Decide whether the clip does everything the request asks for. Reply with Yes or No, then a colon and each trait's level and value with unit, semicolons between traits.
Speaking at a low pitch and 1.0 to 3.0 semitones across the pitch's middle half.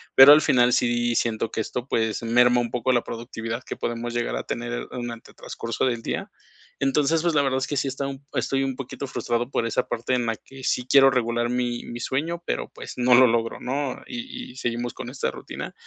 Yes: low, 125 Hz; narrow, 2.4 semitones